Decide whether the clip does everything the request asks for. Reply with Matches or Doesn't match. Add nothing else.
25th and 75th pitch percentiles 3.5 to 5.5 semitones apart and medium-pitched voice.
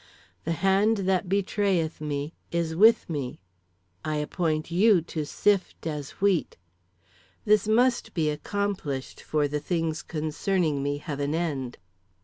Matches